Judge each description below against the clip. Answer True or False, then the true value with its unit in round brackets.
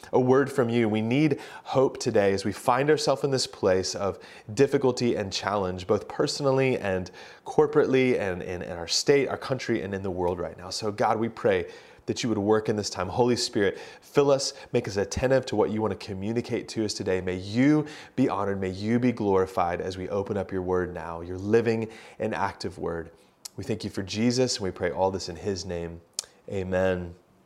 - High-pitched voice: False (110 Hz)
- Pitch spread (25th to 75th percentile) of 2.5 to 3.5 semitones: False (5.4 semitones)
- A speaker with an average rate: False (210 wpm)